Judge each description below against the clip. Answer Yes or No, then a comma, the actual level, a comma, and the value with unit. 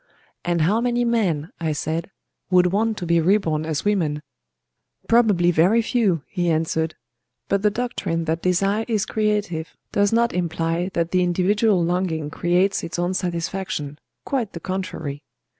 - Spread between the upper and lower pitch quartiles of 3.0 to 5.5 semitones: Yes, average, 3.9 semitones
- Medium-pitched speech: Yes, medium, 180 Hz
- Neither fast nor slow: Yes, average, 145 wpm